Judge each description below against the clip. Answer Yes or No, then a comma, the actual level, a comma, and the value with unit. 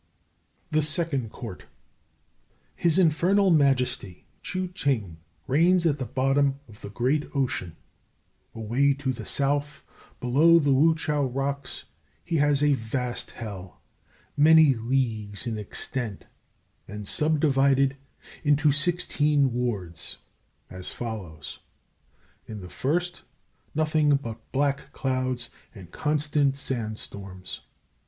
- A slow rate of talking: Yes, slow, 110 wpm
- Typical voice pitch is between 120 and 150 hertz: Yes, low, 135 Hz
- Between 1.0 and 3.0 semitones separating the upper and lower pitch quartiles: No, average, 4.5 semitones